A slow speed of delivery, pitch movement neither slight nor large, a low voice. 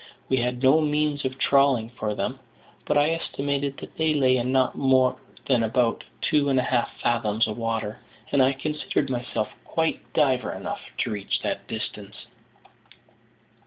No: average, 160 wpm; average, 3.2 semitones; low, 130 Hz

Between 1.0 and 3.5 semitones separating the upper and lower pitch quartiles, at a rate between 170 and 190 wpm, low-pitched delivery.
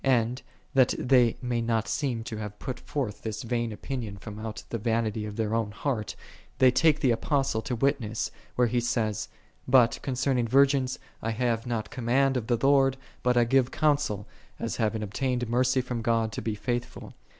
Yes: average, 2.7 semitones; average, 185 wpm; low, 120 Hz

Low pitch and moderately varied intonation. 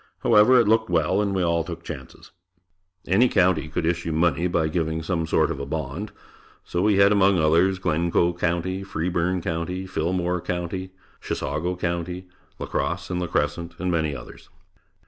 No: very low, 85 Hz; narrow, 2.2 semitones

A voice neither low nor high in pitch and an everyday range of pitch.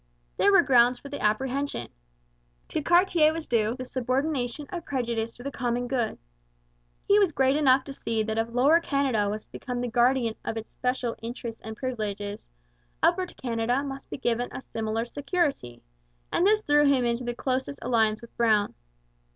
No: high, 245 Hz; average, 3.6 semitones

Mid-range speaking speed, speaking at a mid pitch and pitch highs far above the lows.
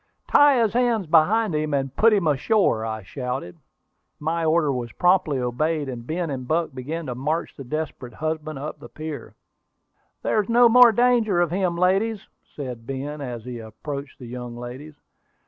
Yes: average, 175 wpm; medium, 155 Hz; wide, 6.1 semitones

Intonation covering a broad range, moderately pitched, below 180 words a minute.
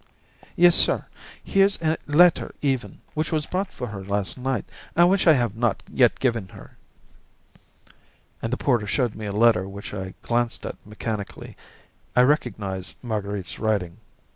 No: wide, 6.3 semitones; low, 115 Hz; average, 155 wpm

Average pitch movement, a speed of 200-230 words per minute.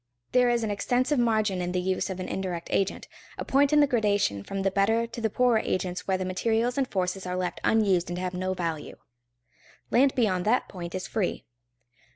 Yes: average, 4.2 semitones; fast, 205 wpm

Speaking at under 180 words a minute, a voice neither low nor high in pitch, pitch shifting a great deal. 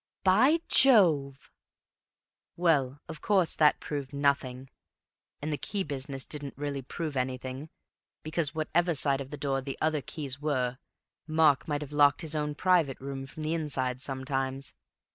No: average, 150 wpm; medium, 145 Hz; average, 2.7 semitones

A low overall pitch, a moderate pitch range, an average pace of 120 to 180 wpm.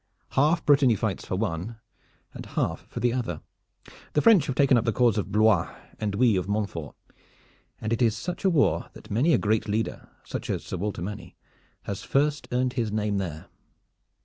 No: low, 110 Hz; average, 4.2 semitones; average, 190 wpm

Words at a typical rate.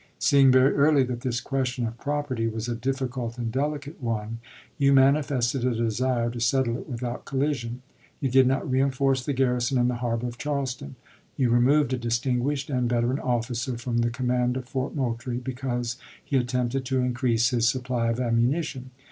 Yes: average, 175 wpm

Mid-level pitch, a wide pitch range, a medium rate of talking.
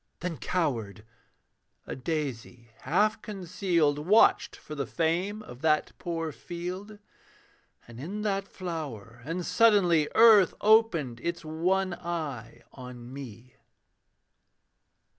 No: medium, 165 Hz; wide, 6.3 semitones; slow, 105 wpm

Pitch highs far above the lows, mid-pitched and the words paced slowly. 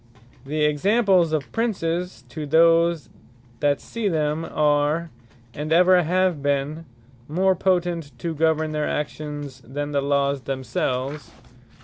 No: average, 2.9 semitones; medium, 155 Hz; slow, 120 wpm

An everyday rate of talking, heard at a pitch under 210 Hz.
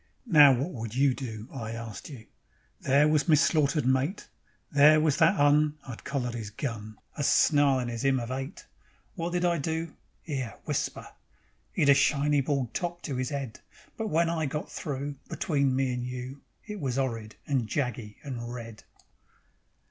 Yes: average, 170 wpm; medium, 140 Hz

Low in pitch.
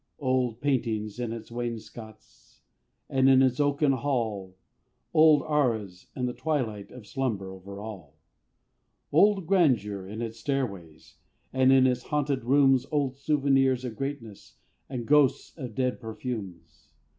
Yes: low, 125 Hz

